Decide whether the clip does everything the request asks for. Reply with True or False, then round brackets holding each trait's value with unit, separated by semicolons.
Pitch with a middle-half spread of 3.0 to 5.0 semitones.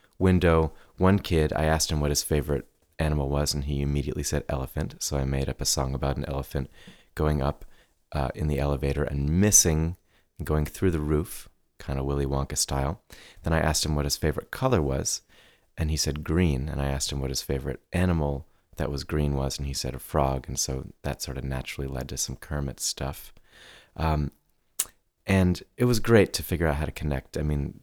False (2.6 semitones)